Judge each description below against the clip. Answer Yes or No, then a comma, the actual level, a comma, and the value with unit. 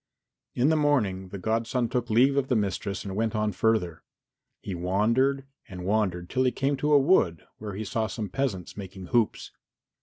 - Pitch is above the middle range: No, low, 110 Hz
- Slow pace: No, average, 185 wpm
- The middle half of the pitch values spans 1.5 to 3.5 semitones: No, average, 5.2 semitones